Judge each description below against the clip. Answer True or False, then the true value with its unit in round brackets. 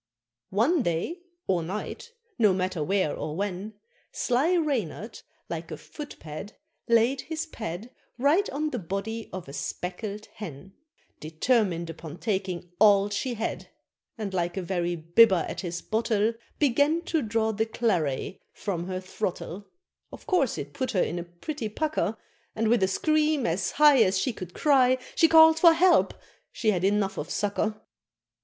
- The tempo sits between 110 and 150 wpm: False (160 wpm)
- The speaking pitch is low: False (210 Hz)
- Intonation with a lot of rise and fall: True (6.3 semitones)